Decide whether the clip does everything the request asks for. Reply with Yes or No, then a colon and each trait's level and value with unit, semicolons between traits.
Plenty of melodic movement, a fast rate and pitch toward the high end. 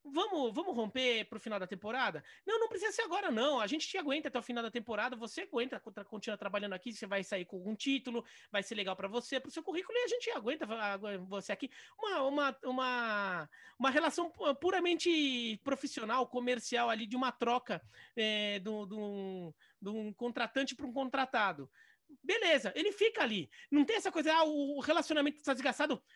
Yes: wide, 6.1 semitones; fast, 195 wpm; very high, 255 Hz